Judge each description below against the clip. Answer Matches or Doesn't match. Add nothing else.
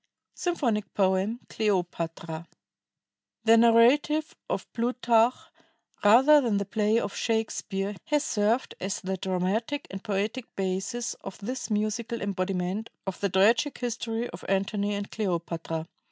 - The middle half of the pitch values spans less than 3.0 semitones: Doesn't match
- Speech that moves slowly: Matches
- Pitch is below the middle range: Doesn't match